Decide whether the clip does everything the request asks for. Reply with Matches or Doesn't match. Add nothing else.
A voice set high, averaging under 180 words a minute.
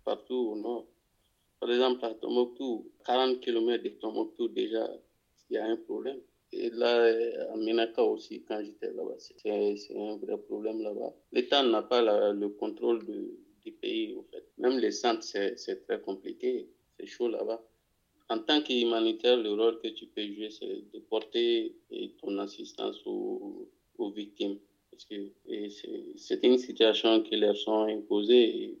Matches